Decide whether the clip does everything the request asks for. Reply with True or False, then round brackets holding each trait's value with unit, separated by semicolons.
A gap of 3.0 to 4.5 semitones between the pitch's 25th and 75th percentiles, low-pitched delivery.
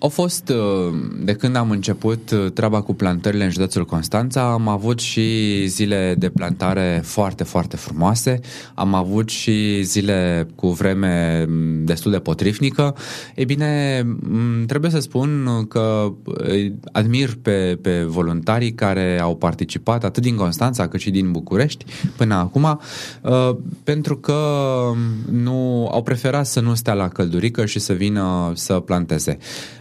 False (4.9 semitones; 105 Hz)